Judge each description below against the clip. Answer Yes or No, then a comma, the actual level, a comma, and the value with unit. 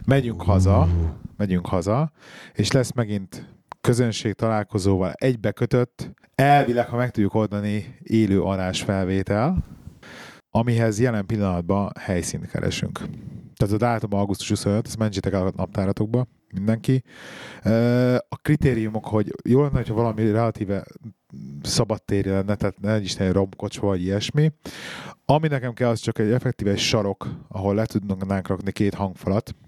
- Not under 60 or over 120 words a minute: No, average, 135 wpm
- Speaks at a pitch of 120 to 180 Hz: No, low, 110 Hz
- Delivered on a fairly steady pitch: No, average, 3.5 semitones